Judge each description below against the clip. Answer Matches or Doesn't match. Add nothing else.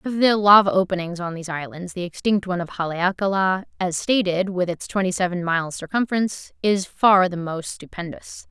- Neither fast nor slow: Matches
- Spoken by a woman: Matches